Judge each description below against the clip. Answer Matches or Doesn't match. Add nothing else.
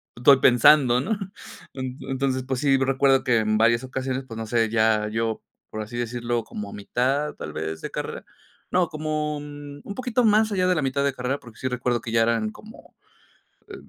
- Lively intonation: Doesn't match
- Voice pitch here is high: Doesn't match